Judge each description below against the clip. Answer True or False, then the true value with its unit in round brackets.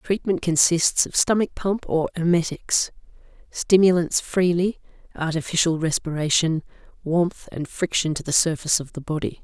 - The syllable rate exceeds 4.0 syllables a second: True (4.8 syllables/s)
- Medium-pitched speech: True (165 Hz)